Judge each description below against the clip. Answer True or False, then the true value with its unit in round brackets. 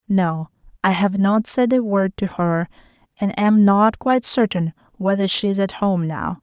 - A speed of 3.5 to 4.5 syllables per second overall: True (4.4 syllables/s)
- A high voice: True (195 Hz)